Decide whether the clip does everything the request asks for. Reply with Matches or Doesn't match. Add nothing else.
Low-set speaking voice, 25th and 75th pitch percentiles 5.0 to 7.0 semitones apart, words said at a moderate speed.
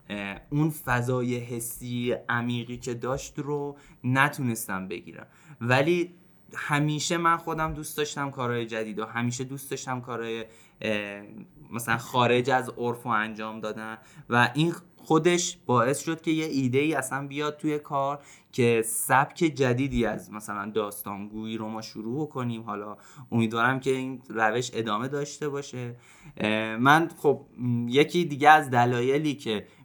Doesn't match